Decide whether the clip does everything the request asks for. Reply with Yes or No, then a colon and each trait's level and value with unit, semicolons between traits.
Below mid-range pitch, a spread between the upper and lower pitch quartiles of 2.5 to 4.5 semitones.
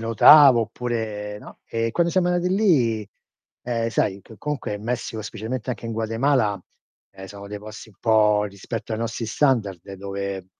Yes: low, 115 Hz; average, 2.9 semitones